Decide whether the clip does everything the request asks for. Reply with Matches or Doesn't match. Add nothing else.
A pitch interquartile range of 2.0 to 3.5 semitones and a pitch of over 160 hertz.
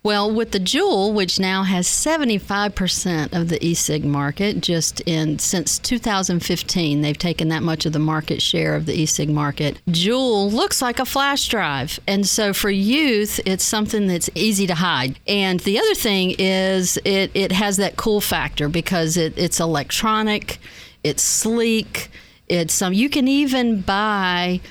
Doesn't match